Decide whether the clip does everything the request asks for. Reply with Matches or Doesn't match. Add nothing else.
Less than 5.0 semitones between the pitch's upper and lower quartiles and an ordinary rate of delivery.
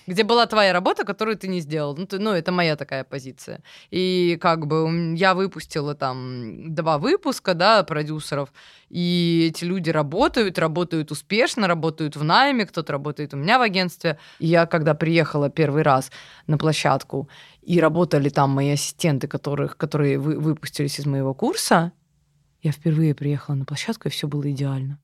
Doesn't match